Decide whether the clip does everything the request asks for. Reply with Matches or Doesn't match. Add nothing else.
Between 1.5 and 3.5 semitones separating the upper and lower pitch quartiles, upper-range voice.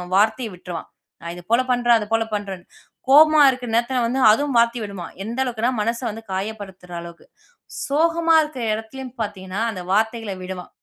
Doesn't match